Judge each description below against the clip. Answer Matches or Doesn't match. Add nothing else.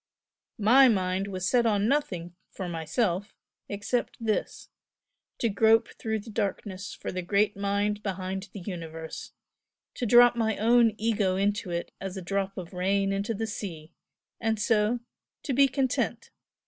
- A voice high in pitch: Matches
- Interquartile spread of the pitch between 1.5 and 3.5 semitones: Matches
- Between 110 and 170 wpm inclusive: Matches